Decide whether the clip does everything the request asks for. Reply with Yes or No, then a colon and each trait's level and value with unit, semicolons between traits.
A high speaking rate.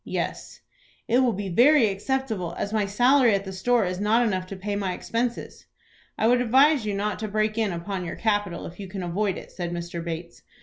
Yes: fast, 215 wpm